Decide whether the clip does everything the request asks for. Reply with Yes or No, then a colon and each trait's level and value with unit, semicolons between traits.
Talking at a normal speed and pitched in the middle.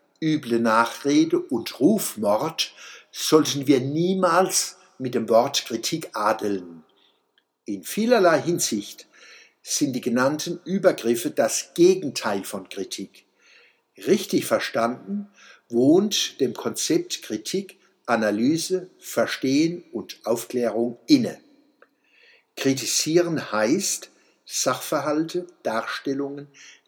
No: slow, 85 wpm; medium, 160 Hz